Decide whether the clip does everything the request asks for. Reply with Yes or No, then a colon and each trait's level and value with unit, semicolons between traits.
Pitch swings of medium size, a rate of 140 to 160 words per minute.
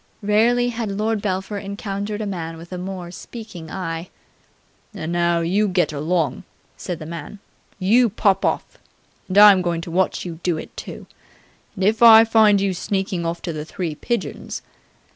No: average, 3.5 semitones; average, 170 wpm